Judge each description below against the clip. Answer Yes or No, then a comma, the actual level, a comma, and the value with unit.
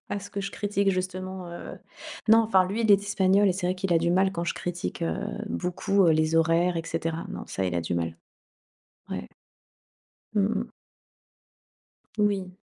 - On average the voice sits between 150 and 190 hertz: Yes, medium, 185 Hz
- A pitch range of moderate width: Yes, average, 3.0 semitones